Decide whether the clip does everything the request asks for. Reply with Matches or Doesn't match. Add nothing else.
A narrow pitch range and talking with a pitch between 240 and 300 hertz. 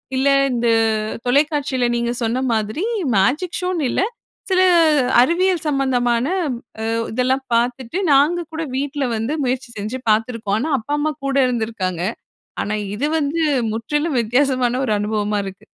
Doesn't match